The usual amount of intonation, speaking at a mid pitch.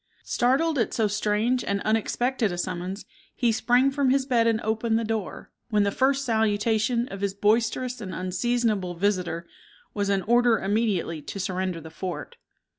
No: average, 3.7 semitones; high, 220 Hz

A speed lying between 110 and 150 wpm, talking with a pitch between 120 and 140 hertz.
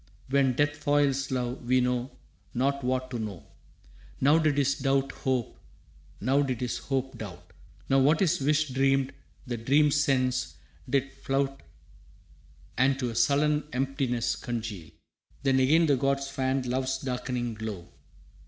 Yes: average, 145 wpm; low, 135 Hz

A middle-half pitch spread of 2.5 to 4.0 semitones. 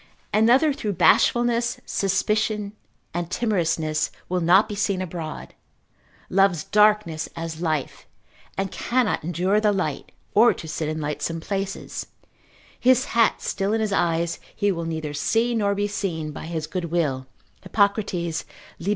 No: average, 4.5 semitones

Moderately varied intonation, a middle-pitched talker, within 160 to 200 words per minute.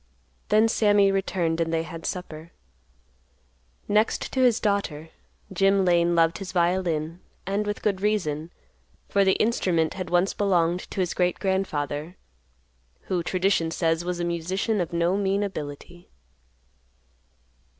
No: average, 3.0 semitones; medium, 180 Hz; slow, 135 wpm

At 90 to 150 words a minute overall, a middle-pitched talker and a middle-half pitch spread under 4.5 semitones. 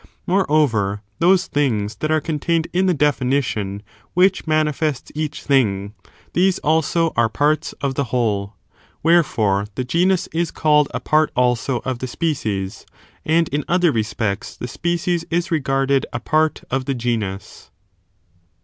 No: average, 140 wpm; medium, 145 Hz; wide, 5.6 semitones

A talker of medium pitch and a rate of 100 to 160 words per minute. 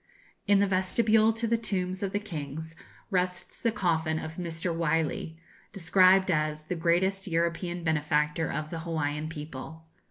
Yes: medium, 170 Hz; average, 150 wpm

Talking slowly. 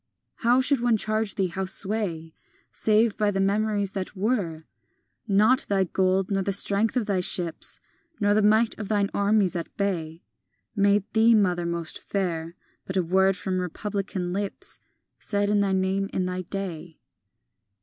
No: average, 165 wpm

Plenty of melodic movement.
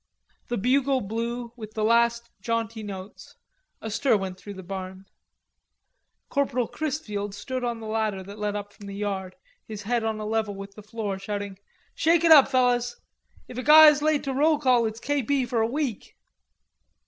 No: average, 3.9 semitones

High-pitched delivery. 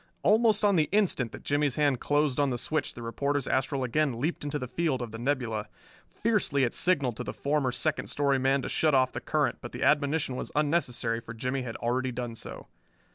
No: low, 135 Hz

